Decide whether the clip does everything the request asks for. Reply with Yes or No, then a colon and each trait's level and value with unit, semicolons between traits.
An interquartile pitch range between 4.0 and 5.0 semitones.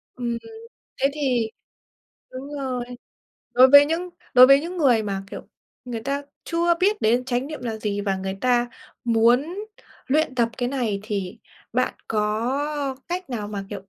Yes: average, 4.4 semitones